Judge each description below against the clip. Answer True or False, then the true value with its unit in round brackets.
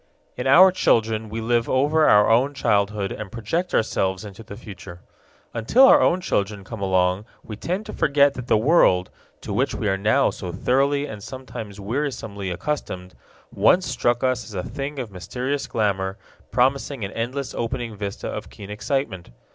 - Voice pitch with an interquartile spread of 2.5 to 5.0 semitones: False (5.4 semitones)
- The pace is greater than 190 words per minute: False (170 wpm)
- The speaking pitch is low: True (115 Hz)